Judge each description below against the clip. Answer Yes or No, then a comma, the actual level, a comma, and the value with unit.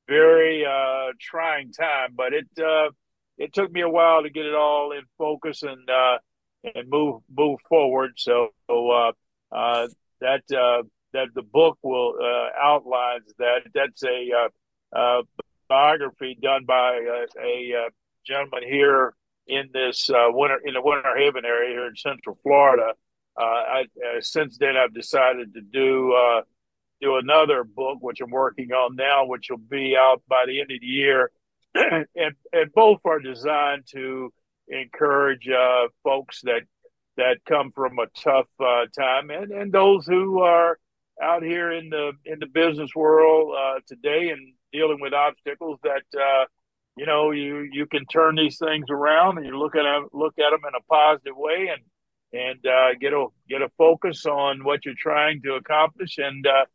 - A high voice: No, medium, 140 Hz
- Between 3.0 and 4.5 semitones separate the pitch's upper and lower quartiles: Yes, average, 3.4 semitones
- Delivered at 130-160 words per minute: No, average, 170 wpm